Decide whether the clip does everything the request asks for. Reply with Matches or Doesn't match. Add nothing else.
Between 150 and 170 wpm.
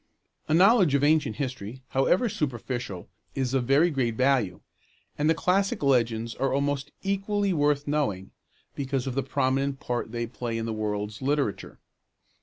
Matches